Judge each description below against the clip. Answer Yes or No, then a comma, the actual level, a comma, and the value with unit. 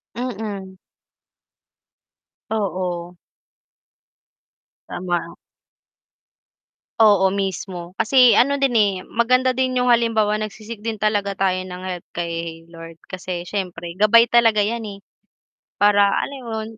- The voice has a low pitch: No, high, 205 Hz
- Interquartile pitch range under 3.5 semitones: No, average, 3.9 semitones